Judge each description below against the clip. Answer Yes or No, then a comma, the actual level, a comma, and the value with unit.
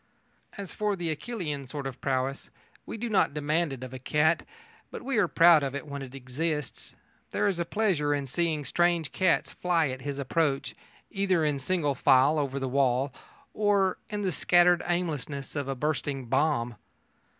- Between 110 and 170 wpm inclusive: No, average, 180 wpm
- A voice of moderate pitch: Yes, medium, 150 Hz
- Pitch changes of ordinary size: Yes, average, 4.3 semitones